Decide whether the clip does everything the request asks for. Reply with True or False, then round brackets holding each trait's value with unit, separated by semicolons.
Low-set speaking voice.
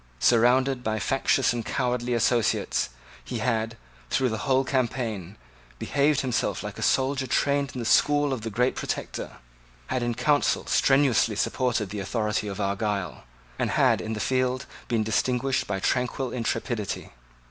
True (120 Hz)